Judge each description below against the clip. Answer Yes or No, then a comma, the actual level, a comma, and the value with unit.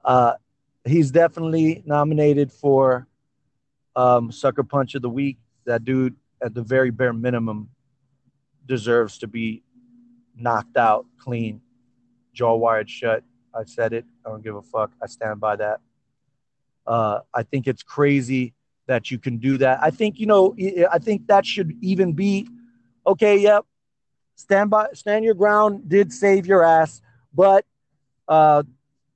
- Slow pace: No, average, 150 wpm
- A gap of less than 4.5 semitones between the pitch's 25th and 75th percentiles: No, average, 5.3 semitones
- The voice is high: No, low, 135 Hz